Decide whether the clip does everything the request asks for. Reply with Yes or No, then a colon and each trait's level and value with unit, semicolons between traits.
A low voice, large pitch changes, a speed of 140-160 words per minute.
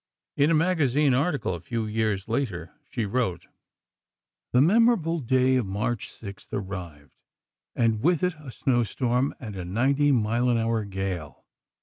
Yes: low, 120 Hz; wide, 5.8 semitones; average, 150 wpm